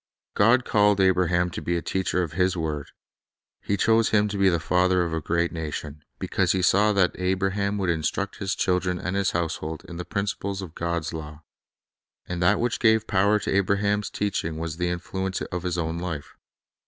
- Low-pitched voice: Yes, very low, 90 Hz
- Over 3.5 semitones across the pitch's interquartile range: No, average, 2.8 semitones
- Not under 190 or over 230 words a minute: Yes, average, 195 wpm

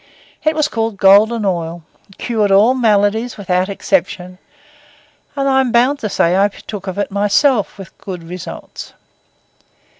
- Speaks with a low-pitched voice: No, high, 205 Hz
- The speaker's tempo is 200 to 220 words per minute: No, average, 150 wpm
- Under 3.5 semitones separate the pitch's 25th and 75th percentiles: No, average, 3.9 semitones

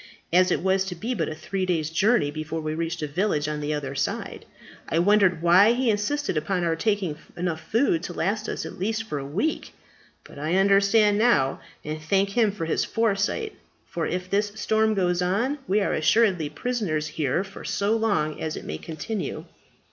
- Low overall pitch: No, medium, 185 Hz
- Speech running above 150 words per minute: Yes, average, 195 wpm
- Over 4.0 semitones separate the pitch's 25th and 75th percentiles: Yes, average, 5.2 semitones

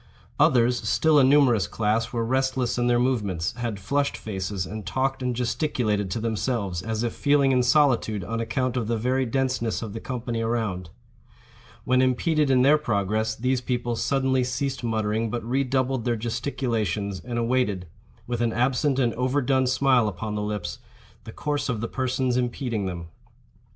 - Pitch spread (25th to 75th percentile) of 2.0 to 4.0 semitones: Yes, average, 3.0 semitones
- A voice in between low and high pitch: No, low, 120 Hz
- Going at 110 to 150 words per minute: No, average, 170 wpm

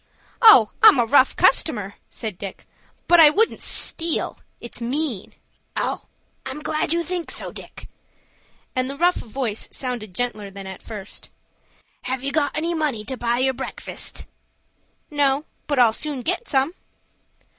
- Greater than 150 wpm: No, average, 145 wpm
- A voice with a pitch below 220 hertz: No, very high, 265 Hz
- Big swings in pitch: No, average, 5.0 semitones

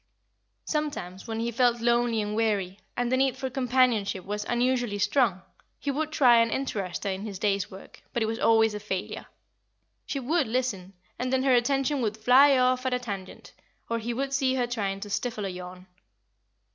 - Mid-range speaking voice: No, high, 235 Hz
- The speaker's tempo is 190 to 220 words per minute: Yes, average, 195 wpm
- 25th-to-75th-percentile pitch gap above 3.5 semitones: Yes, average, 4.0 semitones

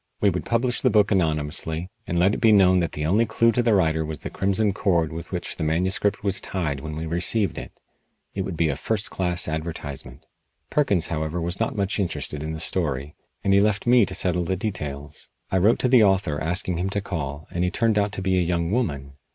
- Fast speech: Yes, fast, 230 wpm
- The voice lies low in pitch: Yes, very low, 90 Hz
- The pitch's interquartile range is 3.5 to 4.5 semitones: Yes, average, 4.2 semitones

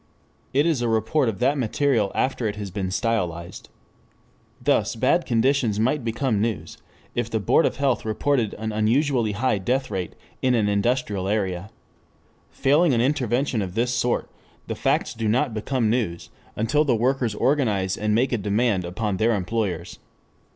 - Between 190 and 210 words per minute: No, average, 165 wpm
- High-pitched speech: No, low, 115 Hz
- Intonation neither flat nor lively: Yes, average, 3.8 semitones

